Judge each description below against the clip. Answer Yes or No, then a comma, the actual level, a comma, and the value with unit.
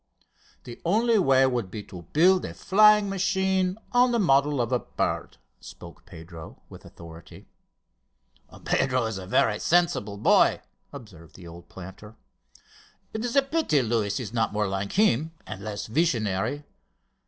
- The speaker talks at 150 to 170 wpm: Yes, average, 155 wpm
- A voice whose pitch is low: Yes, low, 125 Hz